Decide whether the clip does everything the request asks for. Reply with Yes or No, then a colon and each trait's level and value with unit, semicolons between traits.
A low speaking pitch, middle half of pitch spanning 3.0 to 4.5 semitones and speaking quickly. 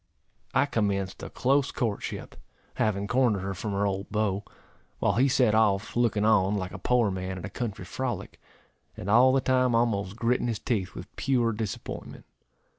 No: low, 110 Hz; average, 3.8 semitones; average, 175 wpm